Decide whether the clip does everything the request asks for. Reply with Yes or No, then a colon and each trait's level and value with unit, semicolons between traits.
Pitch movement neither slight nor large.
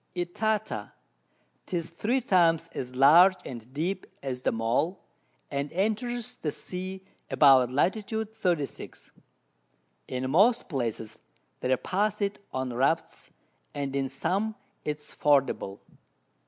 No: wide, 6.9 semitones